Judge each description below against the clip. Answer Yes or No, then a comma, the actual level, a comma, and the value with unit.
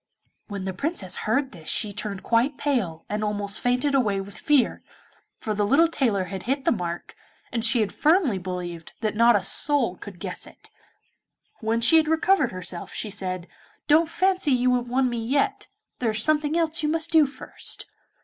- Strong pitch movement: Yes, wide, 6.5 semitones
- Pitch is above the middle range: Yes, high, 230 Hz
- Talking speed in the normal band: Yes, average, 190 wpm